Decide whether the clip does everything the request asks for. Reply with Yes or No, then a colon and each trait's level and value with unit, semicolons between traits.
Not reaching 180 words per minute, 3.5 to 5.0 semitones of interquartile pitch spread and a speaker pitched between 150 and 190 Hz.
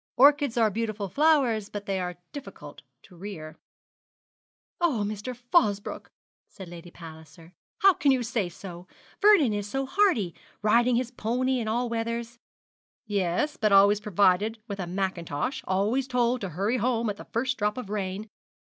No: average, 155 wpm; average, 4.4 semitones; high, 215 Hz